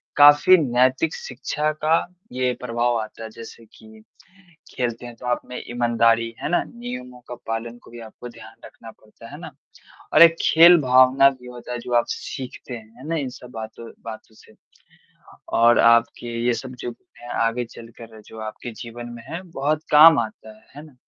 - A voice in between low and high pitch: No, low, 120 Hz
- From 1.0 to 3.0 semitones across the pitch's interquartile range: Yes, average, 2.7 semitones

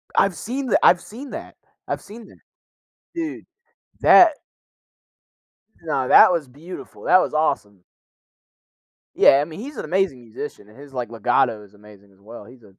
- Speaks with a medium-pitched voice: Yes, medium, 145 Hz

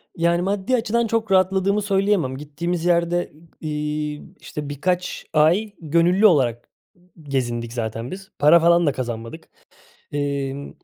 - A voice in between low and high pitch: Yes, medium, 165 Hz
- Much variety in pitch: No, average, 4.7 semitones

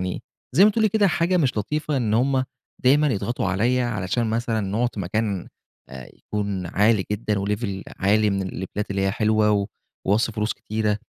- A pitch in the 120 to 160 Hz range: No, low, 110 Hz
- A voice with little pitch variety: No, average, 3.7 semitones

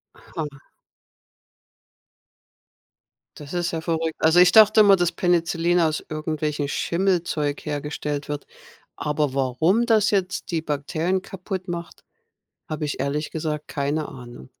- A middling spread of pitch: Yes, average, 3.2 semitones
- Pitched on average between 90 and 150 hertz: No, medium, 160 Hz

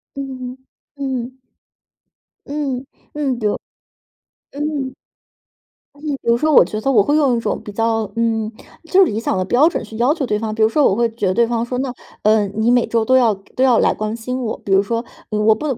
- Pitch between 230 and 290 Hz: Yes, high, 235 Hz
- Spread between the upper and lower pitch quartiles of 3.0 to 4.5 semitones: Yes, average, 3.4 semitones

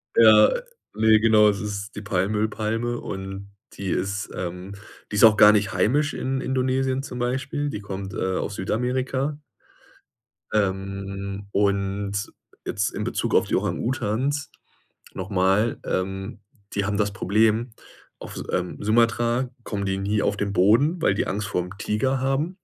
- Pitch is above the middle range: No, low, 105 Hz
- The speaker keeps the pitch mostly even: No, average, 3.5 semitones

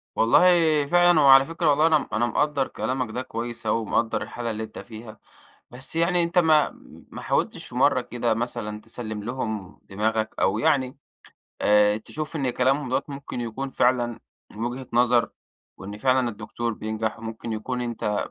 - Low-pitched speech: Yes, low, 120 Hz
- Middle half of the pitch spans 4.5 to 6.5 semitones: No, average, 3.5 semitones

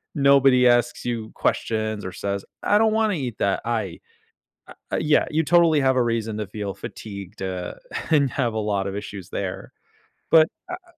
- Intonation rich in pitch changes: Yes, wide, 5.8 semitones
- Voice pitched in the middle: No, low, 115 Hz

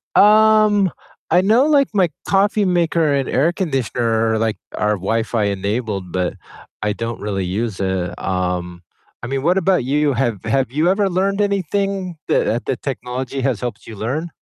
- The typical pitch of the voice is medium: No, low, 130 Hz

